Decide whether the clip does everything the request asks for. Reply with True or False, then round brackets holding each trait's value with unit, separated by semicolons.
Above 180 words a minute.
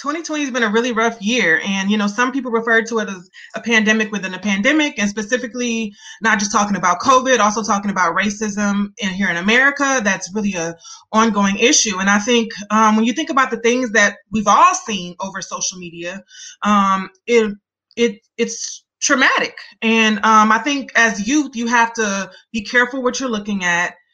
True (195 wpm)